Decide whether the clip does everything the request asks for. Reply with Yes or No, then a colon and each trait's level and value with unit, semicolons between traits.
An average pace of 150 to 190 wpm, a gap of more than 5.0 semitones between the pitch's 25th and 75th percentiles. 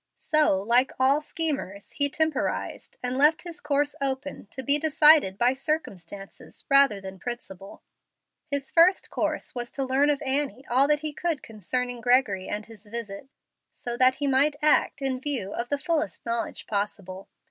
No: average, 165 wpm; average, 4.6 semitones